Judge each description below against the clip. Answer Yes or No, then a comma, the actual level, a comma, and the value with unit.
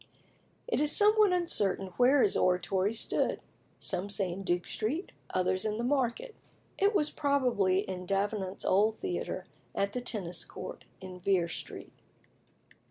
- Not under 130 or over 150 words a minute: Yes, average, 145 wpm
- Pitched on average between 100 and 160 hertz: No, high, 205 Hz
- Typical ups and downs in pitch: No, wide, 7.2 semitones